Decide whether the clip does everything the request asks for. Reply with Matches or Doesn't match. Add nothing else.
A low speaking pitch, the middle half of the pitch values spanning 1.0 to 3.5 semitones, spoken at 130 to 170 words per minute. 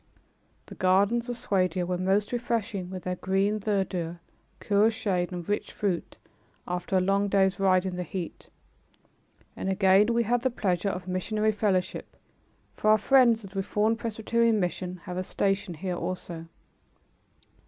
Doesn't match